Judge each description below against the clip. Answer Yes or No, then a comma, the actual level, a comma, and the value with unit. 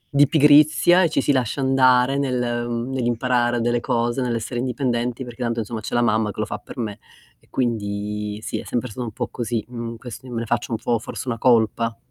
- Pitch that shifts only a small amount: Yes, narrow, 1.8 semitones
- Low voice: Yes, low, 120 Hz